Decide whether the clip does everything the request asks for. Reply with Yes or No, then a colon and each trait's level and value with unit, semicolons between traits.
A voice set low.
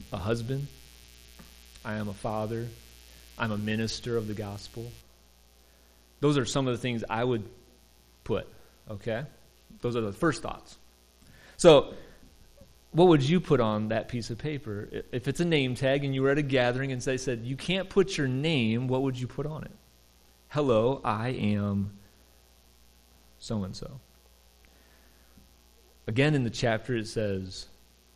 Yes: low, 110 Hz